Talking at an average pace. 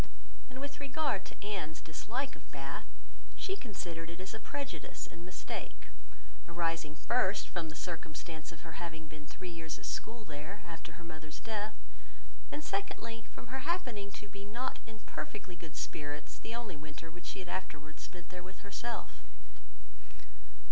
Yes: average, 165 wpm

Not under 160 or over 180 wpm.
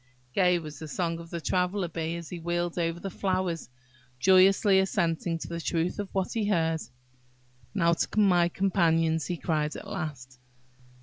Yes: average, 170 wpm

